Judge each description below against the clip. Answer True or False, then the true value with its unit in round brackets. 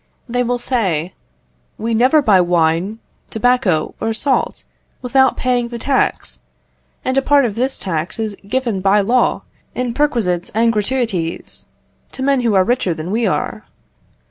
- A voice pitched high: True (230 Hz)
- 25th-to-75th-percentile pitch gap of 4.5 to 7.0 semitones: True (4.9 semitones)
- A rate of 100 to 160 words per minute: True (150 wpm)